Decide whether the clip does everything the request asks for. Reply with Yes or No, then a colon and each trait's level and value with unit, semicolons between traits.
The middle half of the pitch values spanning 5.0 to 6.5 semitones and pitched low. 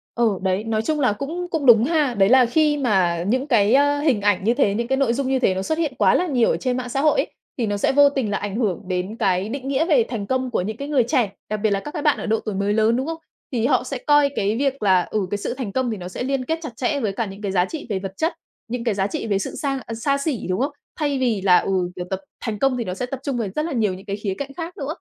No: wide, 5.4 semitones; high, 240 Hz